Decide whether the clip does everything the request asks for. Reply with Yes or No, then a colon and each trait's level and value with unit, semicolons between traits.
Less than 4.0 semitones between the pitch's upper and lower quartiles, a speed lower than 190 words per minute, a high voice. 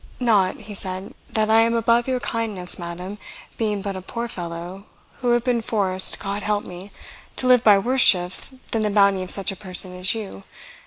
No: average, 3.4 semitones; average, 200 wpm; high, 205 Hz